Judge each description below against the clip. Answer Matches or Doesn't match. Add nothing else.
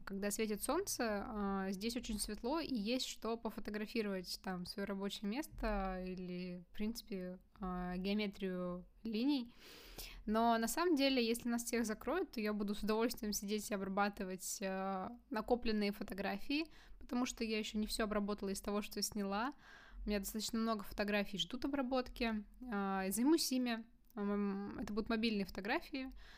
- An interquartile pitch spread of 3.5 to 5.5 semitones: Doesn't match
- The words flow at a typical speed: Matches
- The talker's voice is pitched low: Doesn't match